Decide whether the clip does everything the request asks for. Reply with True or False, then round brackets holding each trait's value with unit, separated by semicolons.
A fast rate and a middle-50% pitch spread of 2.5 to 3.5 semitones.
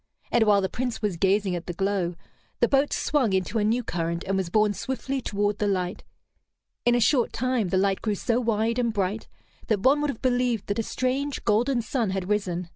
False (215 wpm; 4.2 semitones)